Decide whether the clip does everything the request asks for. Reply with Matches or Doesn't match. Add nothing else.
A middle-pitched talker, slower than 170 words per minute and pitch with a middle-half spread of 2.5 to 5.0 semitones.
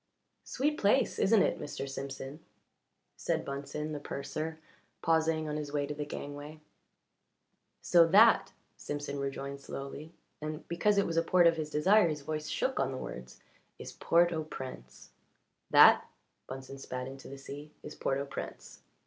Matches